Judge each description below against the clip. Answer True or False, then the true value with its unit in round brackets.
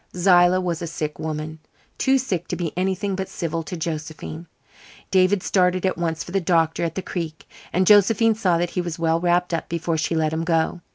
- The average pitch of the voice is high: False (175 Hz)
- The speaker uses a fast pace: True (210 wpm)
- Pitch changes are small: True (2.3 semitones)